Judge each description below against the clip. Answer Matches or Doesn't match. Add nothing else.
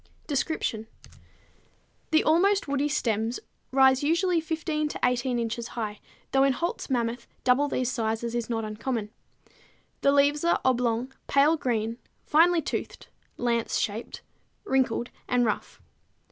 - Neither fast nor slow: Doesn't match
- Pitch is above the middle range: Matches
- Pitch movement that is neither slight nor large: Matches